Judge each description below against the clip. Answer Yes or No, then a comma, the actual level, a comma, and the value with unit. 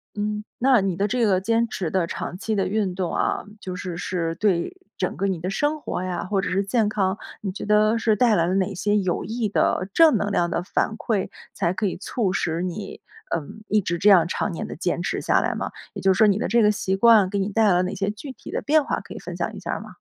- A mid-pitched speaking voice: No, high, 195 Hz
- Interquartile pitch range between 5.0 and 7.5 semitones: No, average, 2.8 semitones